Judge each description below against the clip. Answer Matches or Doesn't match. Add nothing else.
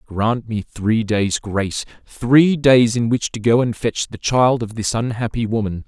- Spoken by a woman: Doesn't match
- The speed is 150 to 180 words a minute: Doesn't match